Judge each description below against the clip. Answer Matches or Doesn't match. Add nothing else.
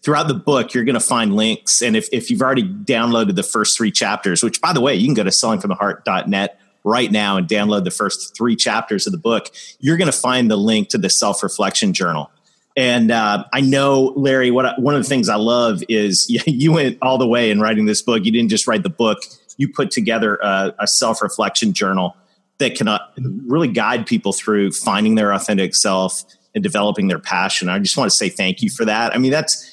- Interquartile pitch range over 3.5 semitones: Matches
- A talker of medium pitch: Doesn't match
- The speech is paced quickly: Matches